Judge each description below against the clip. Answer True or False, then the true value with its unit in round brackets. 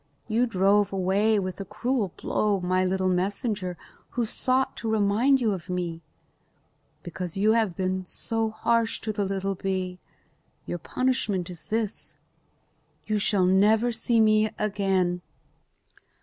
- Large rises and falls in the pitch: False (3.1 semitones)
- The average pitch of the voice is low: False (200 Hz)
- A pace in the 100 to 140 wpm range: True (135 wpm)